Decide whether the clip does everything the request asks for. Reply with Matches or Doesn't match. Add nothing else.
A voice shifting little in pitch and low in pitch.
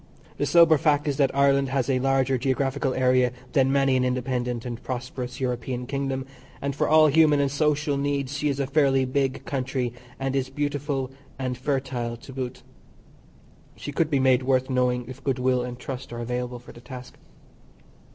Matches